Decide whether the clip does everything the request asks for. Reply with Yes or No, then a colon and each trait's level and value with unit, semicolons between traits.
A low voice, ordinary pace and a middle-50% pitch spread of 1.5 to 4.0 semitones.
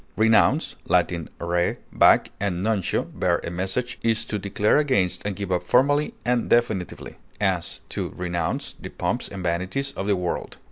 No: low, 100 Hz; average, 160 wpm; average, 4.7 semitones